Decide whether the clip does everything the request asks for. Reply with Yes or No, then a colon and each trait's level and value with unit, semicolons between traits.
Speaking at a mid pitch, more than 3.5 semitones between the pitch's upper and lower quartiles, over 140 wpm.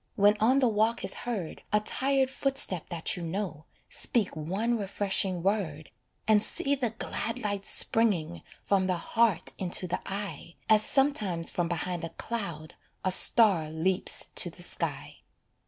No: high, 200 Hz; average, 4.7 semitones; average, 155 wpm